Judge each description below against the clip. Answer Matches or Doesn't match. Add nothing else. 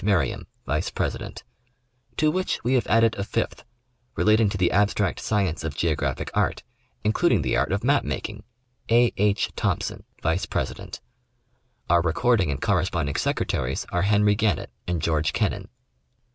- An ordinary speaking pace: Matches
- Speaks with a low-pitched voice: Matches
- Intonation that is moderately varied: Matches